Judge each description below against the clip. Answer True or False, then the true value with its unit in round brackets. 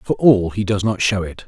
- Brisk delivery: True (285 wpm)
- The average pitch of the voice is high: False (100 Hz)